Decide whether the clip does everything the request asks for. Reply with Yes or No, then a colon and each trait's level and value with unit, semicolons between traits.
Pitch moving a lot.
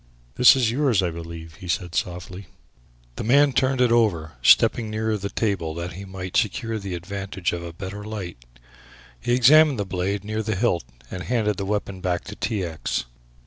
No: average, 4.1 semitones